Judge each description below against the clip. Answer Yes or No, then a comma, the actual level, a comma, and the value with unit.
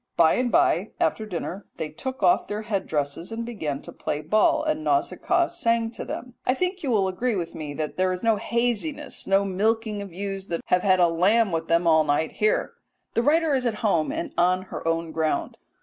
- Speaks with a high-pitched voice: Yes, high, 200 Hz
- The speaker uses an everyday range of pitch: No, wide, 5.8 semitones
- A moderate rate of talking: No, fast, 220 wpm